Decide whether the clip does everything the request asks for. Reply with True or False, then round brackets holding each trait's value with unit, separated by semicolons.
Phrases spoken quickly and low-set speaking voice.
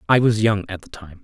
True (290 wpm; 100 Hz)